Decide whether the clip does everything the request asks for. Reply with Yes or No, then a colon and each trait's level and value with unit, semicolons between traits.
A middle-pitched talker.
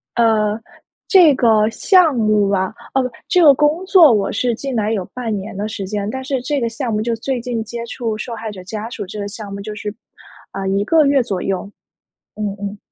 No: high, 225 Hz